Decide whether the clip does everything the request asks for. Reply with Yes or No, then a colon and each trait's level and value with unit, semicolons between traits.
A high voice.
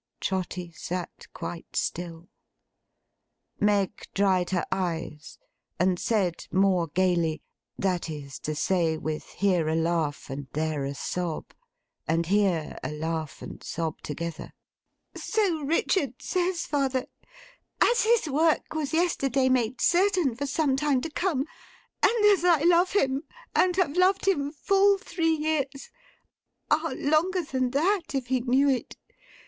Yes: very high, 255 Hz